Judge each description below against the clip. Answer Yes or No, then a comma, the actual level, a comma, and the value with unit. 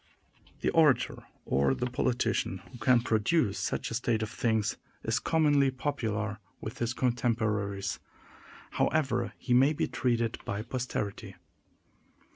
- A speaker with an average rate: No, slow, 125 wpm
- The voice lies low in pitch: Yes, low, 120 Hz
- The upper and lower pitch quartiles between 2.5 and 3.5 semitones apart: Yes, average, 3.1 semitones